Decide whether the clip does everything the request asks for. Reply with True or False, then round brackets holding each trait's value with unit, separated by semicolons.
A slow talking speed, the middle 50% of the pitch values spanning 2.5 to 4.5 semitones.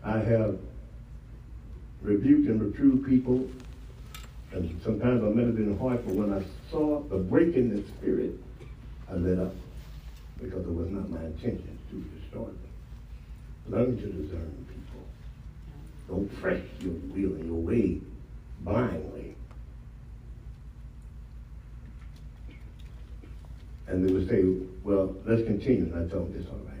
False (130 wpm; 5.6 semitones)